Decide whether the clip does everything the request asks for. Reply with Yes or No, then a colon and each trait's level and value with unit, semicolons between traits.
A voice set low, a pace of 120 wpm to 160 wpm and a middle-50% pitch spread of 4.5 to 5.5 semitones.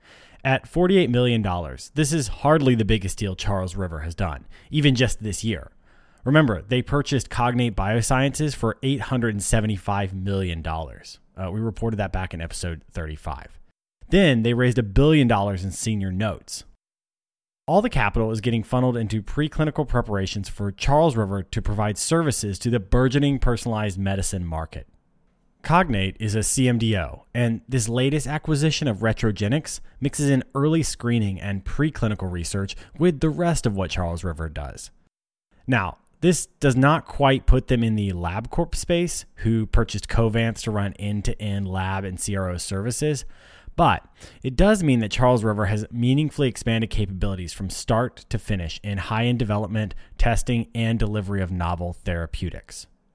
Yes: low, 110 Hz; average, 155 wpm; average, 5.1 semitones